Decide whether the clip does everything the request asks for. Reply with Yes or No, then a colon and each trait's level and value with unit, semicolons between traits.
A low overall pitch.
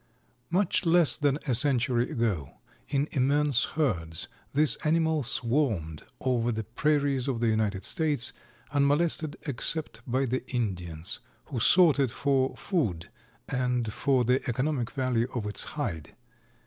Yes: low, 130 Hz